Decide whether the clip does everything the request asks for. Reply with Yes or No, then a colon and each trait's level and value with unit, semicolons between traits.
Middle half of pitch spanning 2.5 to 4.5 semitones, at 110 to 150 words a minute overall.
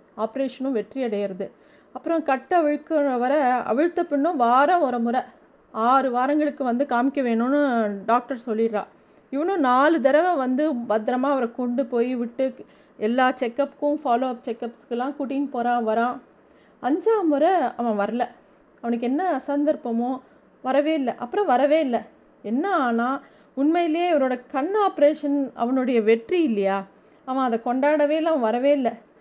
Yes: average, 3.5 semitones; fast, 130 wpm